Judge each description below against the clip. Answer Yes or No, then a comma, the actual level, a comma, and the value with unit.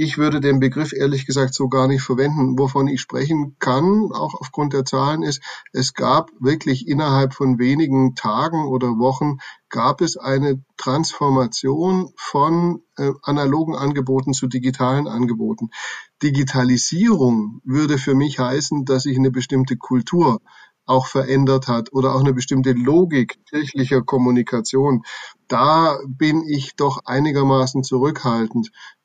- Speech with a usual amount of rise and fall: No, narrow, 2.1 semitones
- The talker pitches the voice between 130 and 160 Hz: Yes, low, 135 Hz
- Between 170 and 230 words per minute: No, average, 135 wpm